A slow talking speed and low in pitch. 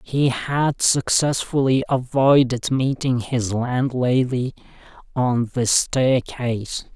Yes: slow, 85 wpm; low, 130 Hz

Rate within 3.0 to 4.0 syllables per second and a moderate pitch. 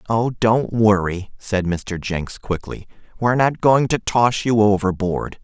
No: 3.9 syllables/s; low, 105 Hz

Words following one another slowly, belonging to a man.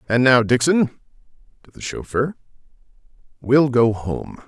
Yes: slow, 120 wpm; male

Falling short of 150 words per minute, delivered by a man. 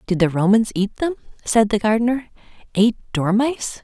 No: average, 140 wpm; female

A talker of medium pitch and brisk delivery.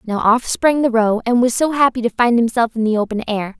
No: high, 235 Hz; fast, 265 wpm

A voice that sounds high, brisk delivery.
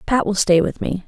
Yes: high, 195 Hz; fast, 280 wpm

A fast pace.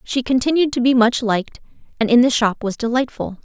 Yes: fast, 210 wpm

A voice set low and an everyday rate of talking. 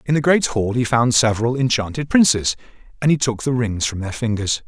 No: low, 120 Hz; fast, 220 wpm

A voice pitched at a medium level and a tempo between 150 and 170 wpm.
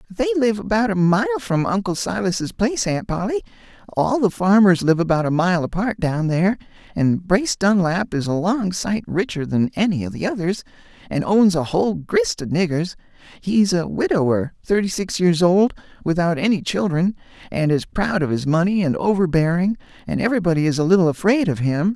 No: medium, 180 Hz; average, 180 wpm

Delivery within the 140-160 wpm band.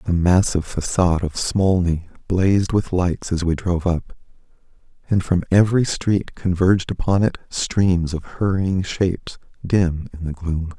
Yes: average, 150 wpm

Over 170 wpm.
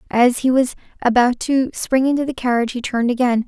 Yes: fast, 205 wpm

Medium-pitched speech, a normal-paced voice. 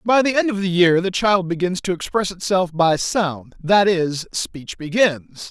Yes: medium, 180 Hz; average, 185 wpm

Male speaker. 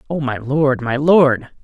Yes: male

